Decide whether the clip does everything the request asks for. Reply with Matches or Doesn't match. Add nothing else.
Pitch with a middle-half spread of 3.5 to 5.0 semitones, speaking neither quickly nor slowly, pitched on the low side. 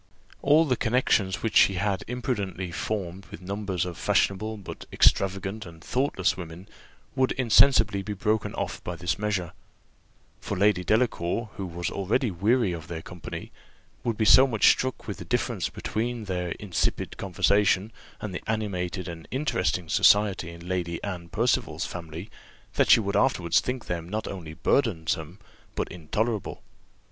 Matches